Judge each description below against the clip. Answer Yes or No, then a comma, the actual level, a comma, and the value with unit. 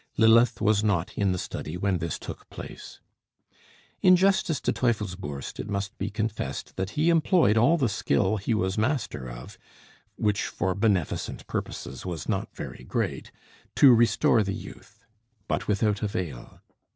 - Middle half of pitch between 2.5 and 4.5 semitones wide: Yes, average, 3.7 semitones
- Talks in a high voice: No, low, 105 Hz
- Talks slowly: No, average, 150 wpm